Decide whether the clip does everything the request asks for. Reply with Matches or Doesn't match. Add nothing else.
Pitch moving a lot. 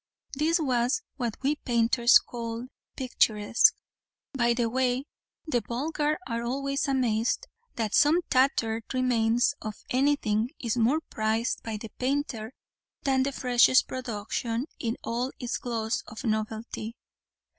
Doesn't match